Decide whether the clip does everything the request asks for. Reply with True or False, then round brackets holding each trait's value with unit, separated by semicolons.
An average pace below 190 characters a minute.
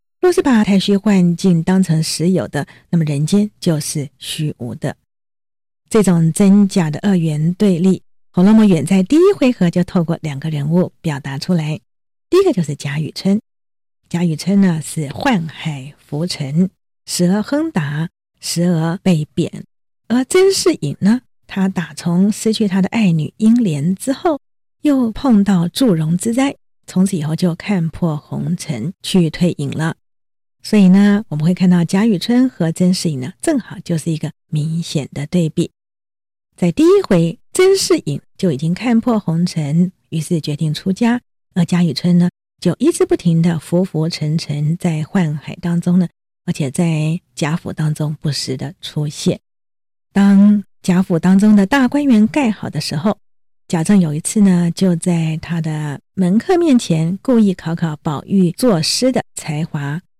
False (230 characters per minute)